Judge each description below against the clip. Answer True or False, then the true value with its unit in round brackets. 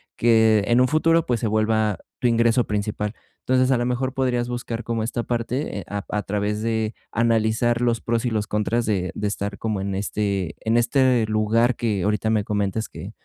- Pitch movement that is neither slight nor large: False (2.3 semitones)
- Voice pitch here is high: False (110 Hz)